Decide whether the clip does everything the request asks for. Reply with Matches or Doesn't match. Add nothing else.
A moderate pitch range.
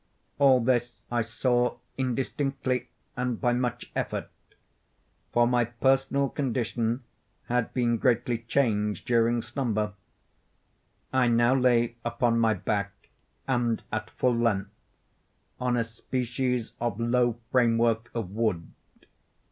Doesn't match